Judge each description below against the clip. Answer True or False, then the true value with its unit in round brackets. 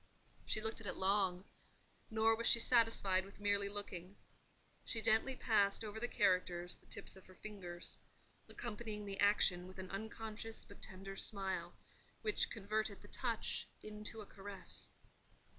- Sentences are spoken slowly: False (150 wpm)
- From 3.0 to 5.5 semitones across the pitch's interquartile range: False (2.4 semitones)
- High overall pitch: True (205 Hz)